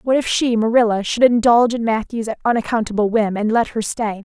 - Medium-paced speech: Yes, average, 180 wpm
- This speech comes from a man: No, female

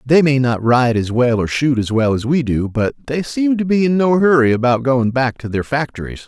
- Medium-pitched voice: No, low, 130 Hz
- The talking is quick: Yes, fast, 260 wpm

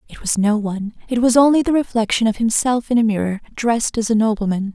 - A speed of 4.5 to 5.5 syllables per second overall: No, 6.3 syllables/s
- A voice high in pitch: Yes, high, 225 Hz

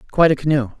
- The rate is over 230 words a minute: No, fast, 225 wpm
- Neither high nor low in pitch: Yes, medium, 145 Hz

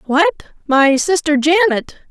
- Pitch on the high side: Yes, very high, 305 Hz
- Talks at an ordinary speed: No, slow, 115 wpm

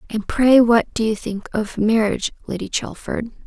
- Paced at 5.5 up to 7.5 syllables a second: No, 4.7 syllables/s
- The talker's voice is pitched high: Yes, high, 225 Hz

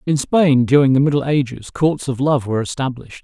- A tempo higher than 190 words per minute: Yes, fast, 205 wpm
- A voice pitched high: No, low, 135 Hz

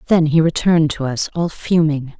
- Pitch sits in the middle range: Yes, medium, 155 Hz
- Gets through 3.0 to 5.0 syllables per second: No, 5.2 syllables/s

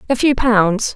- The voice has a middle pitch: No, high, 225 Hz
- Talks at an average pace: Yes, average, 190 wpm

